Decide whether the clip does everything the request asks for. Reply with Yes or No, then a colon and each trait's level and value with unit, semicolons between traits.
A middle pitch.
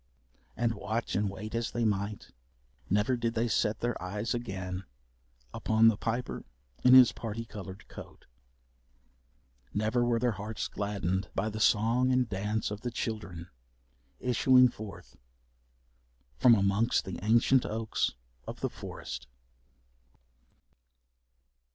No: low, 110 Hz